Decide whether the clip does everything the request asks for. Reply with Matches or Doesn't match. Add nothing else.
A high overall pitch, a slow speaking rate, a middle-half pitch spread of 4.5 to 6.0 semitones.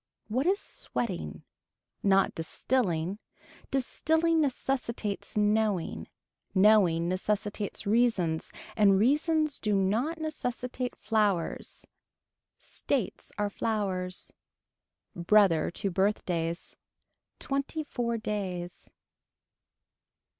Matches